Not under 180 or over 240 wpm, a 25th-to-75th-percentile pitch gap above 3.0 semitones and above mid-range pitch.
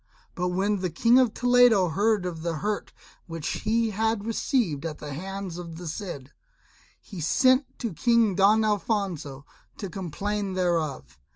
No: average, 155 wpm; average, 4.8 semitones; high, 195 Hz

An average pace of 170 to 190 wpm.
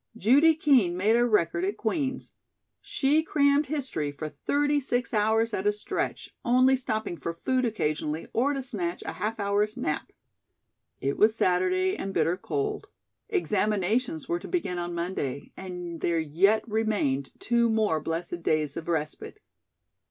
No: average, 150 wpm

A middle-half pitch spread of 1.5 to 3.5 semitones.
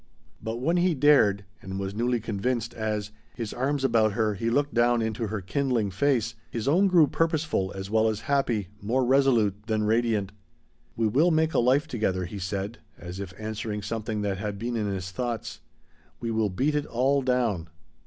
No: average, 4.0 semitones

